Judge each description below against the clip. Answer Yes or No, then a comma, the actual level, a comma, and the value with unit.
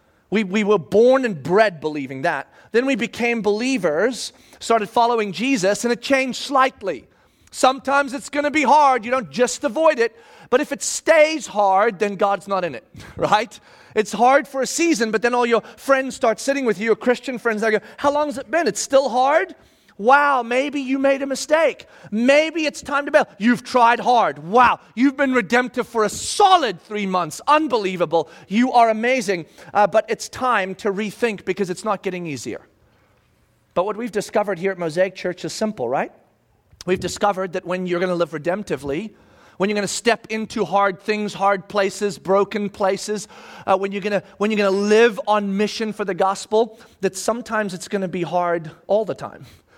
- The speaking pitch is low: No, high, 220 Hz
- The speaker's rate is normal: Yes, average, 190 wpm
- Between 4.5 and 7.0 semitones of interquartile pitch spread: Yes, average, 4.8 semitones